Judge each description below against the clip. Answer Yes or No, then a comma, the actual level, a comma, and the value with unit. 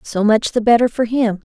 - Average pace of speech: No, fast, 240 wpm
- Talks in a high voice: Yes, high, 225 Hz